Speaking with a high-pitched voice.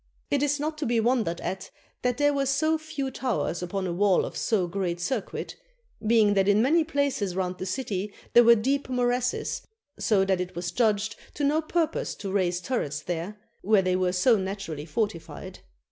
Yes: high, 210 Hz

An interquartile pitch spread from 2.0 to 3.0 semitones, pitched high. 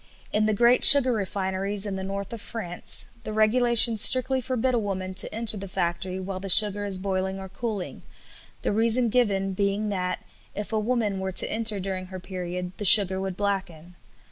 Yes: average, 2.7 semitones; high, 200 Hz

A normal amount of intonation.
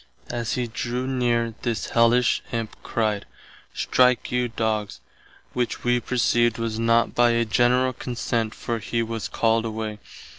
No: narrow, 1.4 semitones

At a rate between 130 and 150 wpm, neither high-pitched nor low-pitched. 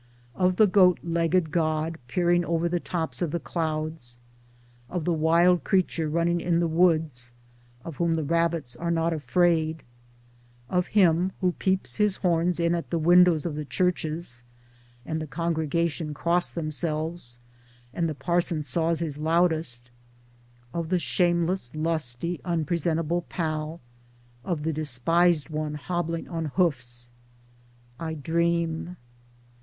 Yes: average, 140 wpm; medium, 165 Hz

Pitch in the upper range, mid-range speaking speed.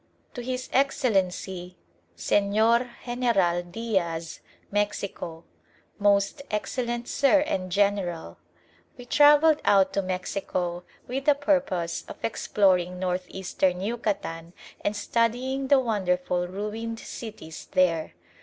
No: high, 200 Hz; slow, 105 wpm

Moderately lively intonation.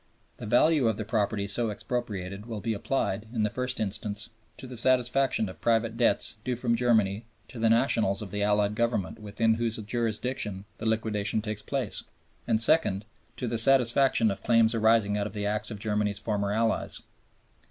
No: narrow, 2.3 semitones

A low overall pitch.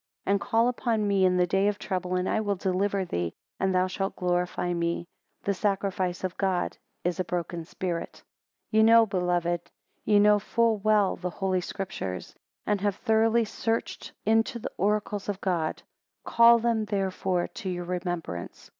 No: high, 190 Hz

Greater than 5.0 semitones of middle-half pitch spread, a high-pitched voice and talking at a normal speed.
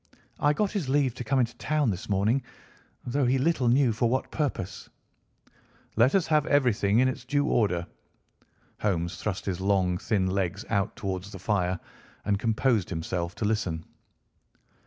No: wide, 5.5 semitones; low, 110 Hz; average, 160 wpm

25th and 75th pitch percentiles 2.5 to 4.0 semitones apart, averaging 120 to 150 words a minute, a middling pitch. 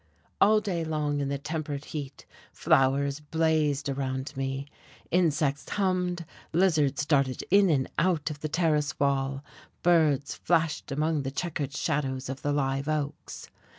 Yes: average, 2.8 semitones; average, 140 wpm; medium, 145 Hz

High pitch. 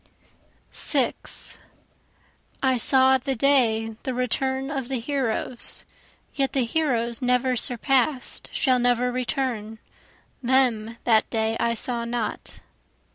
Yes: very high, 250 Hz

